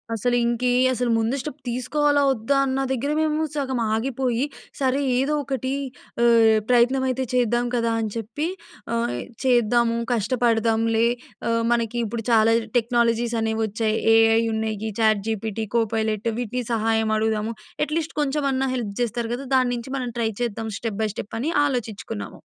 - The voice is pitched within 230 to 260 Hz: Yes, high, 235 Hz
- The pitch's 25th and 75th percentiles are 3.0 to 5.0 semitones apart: No, narrow, 2.4 semitones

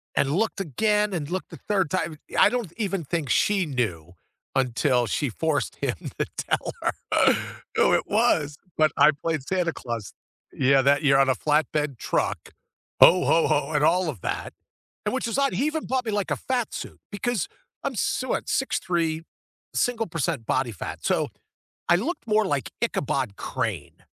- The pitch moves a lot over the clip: Yes, wide, 7.1 semitones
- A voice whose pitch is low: No, medium, 160 Hz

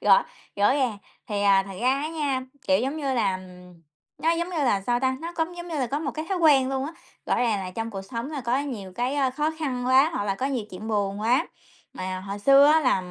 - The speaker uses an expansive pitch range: Yes, wide, 6.0 semitones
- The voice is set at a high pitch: Yes, very high, 260 Hz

